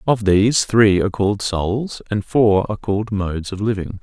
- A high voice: No, low, 105 Hz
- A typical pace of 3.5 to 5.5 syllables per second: Yes, 5.3 syllables/s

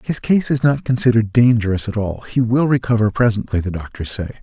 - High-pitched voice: No, low, 115 Hz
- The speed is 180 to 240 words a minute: Yes, fast, 205 wpm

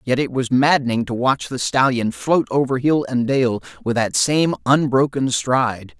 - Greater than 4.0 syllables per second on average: Yes, 4.5 syllables/s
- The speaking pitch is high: No, low, 125 Hz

